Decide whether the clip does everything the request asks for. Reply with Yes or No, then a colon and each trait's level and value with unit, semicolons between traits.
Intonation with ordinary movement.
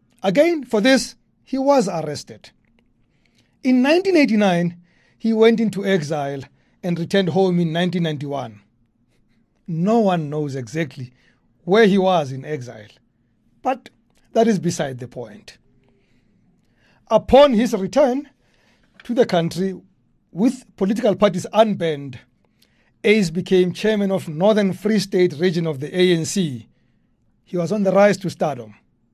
No: wide, 5.9 semitones